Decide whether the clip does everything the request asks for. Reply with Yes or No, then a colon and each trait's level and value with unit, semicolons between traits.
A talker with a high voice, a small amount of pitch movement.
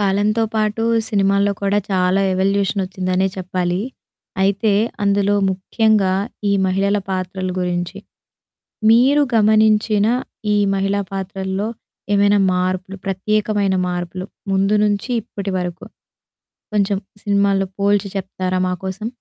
Yes: high, 195 Hz; narrow, 1.6 semitones